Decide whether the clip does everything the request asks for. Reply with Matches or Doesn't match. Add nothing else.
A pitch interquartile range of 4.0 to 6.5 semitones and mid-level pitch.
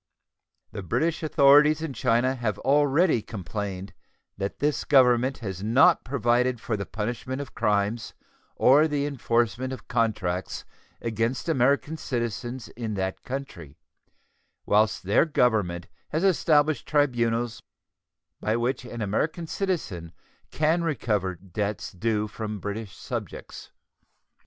Doesn't match